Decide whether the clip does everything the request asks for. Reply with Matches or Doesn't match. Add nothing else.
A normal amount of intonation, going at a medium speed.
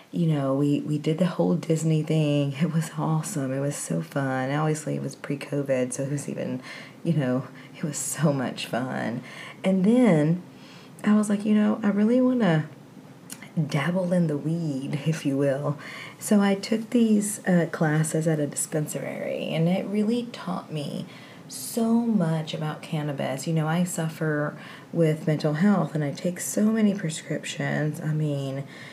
Matches